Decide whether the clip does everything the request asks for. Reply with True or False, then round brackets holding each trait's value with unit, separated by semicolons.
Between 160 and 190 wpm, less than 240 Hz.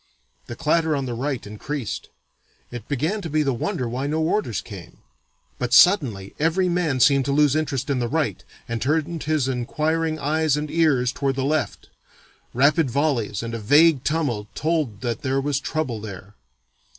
True (175 wpm; 140 Hz)